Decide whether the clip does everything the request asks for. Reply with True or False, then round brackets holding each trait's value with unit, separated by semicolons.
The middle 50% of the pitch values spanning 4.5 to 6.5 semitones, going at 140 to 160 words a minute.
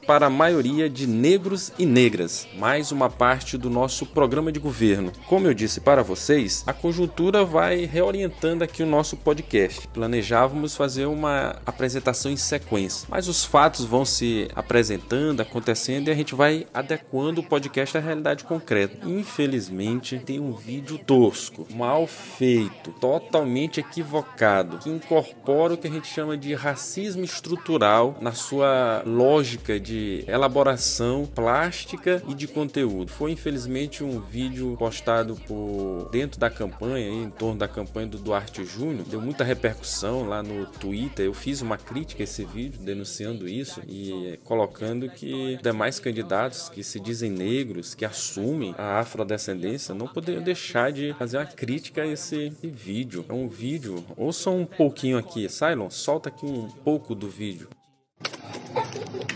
True (5.2 semitones; 150 wpm)